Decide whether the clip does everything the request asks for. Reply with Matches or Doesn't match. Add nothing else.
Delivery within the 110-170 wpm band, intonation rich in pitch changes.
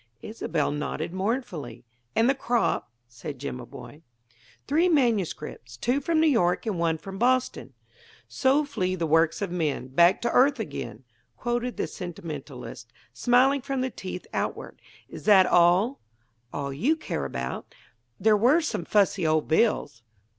Matches